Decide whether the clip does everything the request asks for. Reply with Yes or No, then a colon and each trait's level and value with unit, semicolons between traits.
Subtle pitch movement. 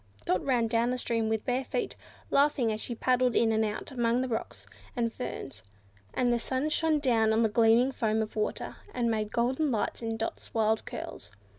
Yes: narrow, 2.3 semitones